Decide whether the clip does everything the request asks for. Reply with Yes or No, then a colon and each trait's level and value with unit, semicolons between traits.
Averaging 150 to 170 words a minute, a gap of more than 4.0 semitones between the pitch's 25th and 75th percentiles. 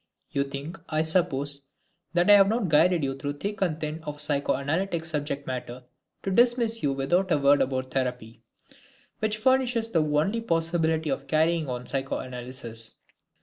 Yes: average, 155 wpm; average, 4.8 semitones